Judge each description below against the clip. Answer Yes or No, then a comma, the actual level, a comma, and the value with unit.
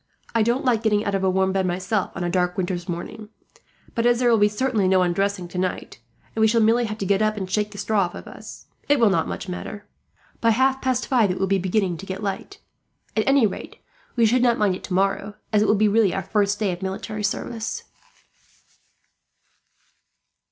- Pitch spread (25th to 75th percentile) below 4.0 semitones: Yes, average, 2.9 semitones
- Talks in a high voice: Yes, high, 205 Hz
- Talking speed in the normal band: No, fast, 215 wpm